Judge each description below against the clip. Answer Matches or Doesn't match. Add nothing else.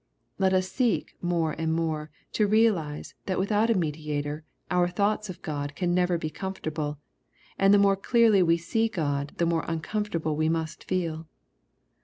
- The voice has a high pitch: Doesn't match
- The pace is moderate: Matches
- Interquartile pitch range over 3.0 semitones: Matches